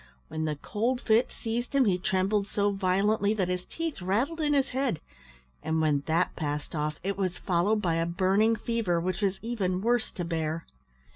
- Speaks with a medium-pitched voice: No, high, 195 Hz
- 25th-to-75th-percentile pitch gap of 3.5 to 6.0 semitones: Yes, average, 4.8 semitones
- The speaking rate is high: No, average, 190 wpm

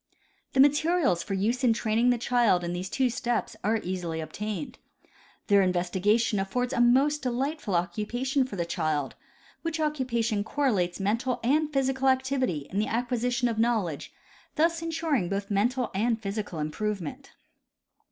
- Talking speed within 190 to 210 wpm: No, average, 155 wpm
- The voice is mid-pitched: No, high, 230 Hz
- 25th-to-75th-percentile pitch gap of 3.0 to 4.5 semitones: No, average, 5.0 semitones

